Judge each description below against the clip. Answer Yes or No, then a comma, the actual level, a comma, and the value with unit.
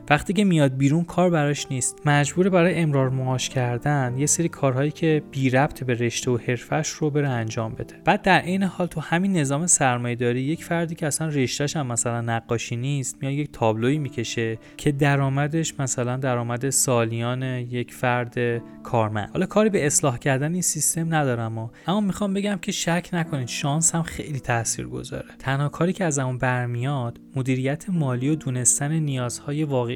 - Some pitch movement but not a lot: Yes, average, 4.5 semitones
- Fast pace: Yes, fast, 170 wpm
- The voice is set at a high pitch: No, medium, 140 Hz